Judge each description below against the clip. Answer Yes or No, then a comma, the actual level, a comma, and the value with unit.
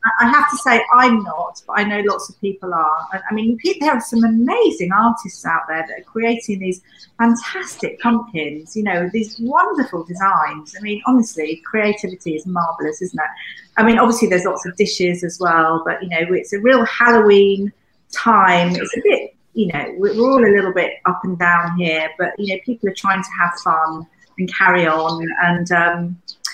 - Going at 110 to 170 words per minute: No, average, 195 wpm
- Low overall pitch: No, high, 195 Hz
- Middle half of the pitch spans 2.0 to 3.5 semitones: No, average, 4.9 semitones